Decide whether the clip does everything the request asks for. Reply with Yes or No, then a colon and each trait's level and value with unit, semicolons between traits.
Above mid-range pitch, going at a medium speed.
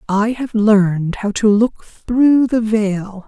Yes: high, 215 Hz; average, 165 wpm